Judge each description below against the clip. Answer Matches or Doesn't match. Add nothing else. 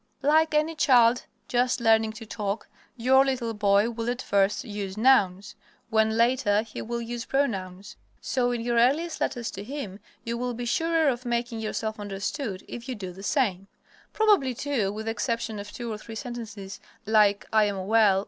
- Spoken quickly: Doesn't match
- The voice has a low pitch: Doesn't match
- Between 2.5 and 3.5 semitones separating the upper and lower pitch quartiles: Matches